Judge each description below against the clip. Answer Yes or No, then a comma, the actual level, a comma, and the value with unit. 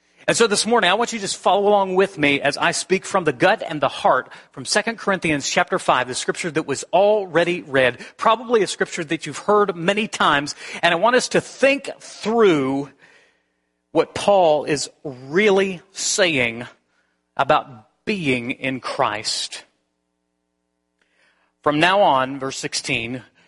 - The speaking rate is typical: Yes, average, 160 wpm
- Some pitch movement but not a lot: No, wide, 7.3 semitones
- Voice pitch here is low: No, medium, 165 Hz